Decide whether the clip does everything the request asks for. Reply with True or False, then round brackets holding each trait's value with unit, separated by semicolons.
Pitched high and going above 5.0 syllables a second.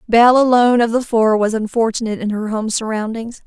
True (225 Hz; 6.1 syllables/s)